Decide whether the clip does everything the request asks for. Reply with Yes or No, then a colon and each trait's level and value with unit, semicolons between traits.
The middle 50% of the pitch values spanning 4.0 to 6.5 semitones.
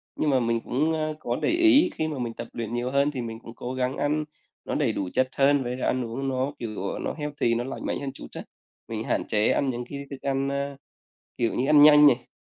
No: average, 3.2 semitones